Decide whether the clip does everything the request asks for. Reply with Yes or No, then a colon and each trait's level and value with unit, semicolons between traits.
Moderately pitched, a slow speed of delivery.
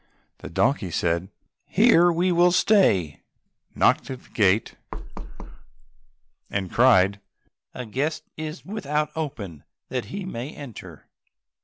No: low, 130 Hz; slow, 115 wpm